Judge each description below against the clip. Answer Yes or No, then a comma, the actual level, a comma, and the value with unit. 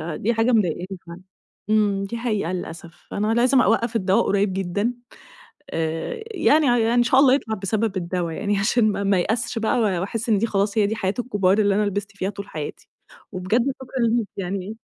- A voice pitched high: Yes, high, 205 Hz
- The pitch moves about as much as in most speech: Yes, average, 3.3 semitones